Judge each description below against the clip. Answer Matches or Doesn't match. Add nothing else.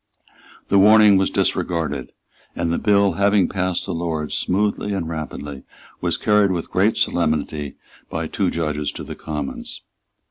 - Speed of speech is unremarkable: Matches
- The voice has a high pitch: Doesn't match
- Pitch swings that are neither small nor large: Matches